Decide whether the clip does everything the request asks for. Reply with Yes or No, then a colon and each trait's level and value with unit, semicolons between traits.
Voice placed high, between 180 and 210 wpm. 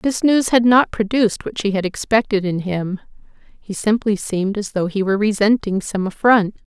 Yes: high, 210 Hz; average, 195 wpm